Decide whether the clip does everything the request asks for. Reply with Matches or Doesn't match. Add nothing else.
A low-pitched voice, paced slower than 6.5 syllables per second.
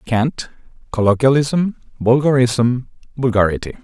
Matches